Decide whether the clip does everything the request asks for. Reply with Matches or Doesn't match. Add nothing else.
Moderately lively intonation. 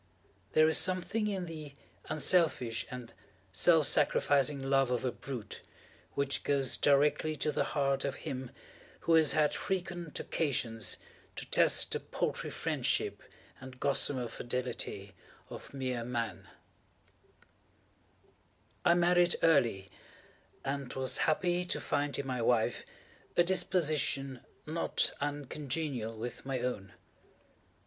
Matches